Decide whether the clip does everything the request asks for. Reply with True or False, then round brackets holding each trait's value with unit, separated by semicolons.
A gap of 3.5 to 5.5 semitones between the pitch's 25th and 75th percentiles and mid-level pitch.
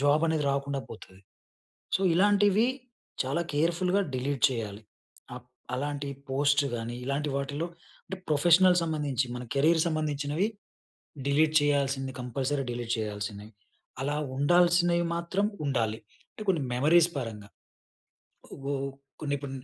True (4.1 semitones; 145 Hz)